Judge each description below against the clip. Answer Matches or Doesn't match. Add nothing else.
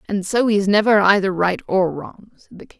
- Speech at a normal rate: Doesn't match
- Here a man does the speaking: Doesn't match